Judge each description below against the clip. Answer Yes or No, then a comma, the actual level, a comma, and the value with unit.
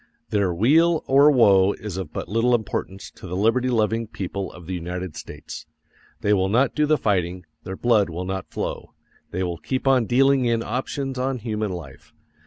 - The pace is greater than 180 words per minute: Yes, average, 190 wpm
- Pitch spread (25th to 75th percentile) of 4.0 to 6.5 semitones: Yes, average, 5.2 semitones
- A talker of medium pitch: No, low, 105 Hz